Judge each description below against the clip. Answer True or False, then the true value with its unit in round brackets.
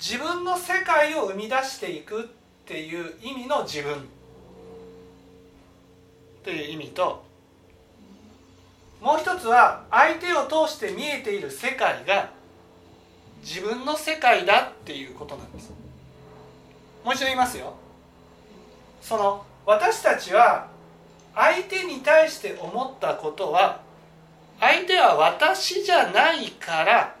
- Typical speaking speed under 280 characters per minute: True (225 characters per minute)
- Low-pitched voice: False (260 Hz)